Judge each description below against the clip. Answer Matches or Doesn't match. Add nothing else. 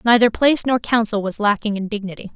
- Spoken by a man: Doesn't match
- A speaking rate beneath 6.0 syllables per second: Doesn't match